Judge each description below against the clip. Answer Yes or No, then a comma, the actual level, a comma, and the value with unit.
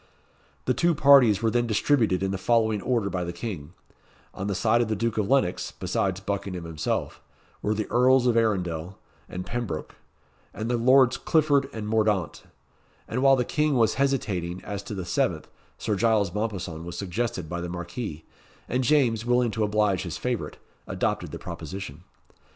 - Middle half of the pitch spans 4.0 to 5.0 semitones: Yes, average, 4.7 semitones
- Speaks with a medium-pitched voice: No, low, 110 Hz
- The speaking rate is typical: Yes, average, 175 wpm